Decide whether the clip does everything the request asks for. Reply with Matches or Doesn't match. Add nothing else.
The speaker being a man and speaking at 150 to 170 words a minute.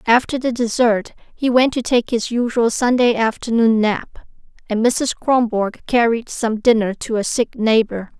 Doesn't match